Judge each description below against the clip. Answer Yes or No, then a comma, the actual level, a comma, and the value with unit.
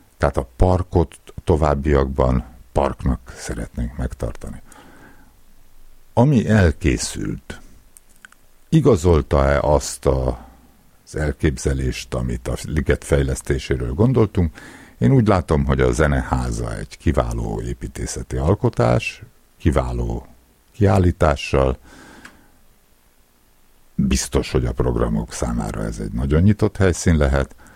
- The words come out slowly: Yes, slow, 90 wpm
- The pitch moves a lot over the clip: Yes, wide, 6.4 semitones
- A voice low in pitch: Yes, very low, 70 Hz